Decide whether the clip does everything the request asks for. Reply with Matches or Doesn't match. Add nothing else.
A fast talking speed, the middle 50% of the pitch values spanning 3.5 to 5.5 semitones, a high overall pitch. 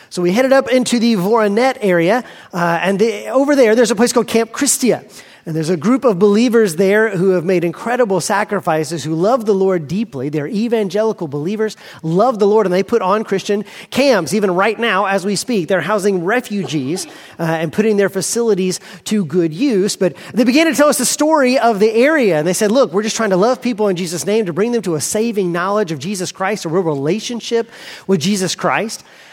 Matches